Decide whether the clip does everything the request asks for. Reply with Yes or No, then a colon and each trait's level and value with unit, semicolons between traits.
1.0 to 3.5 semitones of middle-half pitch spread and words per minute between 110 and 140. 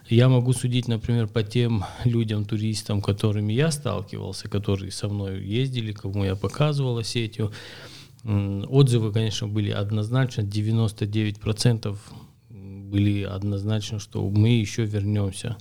Yes: narrow, 2.6 semitones; average, 115 wpm